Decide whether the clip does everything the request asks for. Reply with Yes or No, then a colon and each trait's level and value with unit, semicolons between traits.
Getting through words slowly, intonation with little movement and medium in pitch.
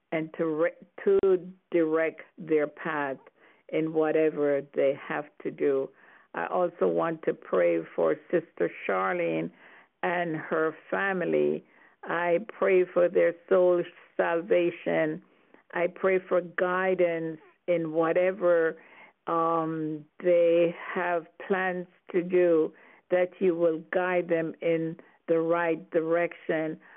Yes: slow, 115 wpm; narrow, 2.0 semitones; medium, 170 Hz